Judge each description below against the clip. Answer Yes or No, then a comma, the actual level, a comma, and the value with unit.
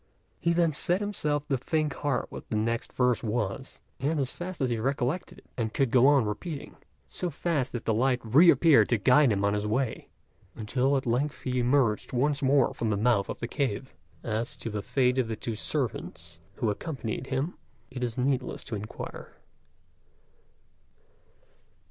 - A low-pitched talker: Yes, low, 125 Hz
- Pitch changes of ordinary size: Yes, average, 4.0 semitones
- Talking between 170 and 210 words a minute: Yes, average, 175 wpm